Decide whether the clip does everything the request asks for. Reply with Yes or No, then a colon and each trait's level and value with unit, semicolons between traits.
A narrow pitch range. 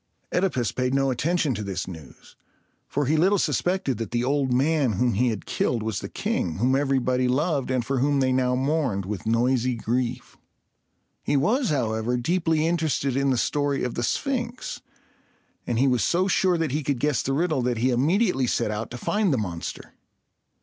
No: average, 4.2 semitones